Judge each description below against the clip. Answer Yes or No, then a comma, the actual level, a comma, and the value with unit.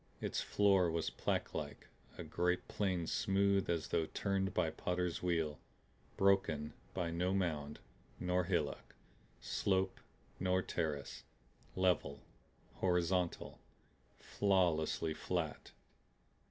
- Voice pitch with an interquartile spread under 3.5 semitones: Yes, average, 2.7 semitones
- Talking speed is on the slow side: Yes, slow, 100 wpm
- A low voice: Yes, very low, 90 Hz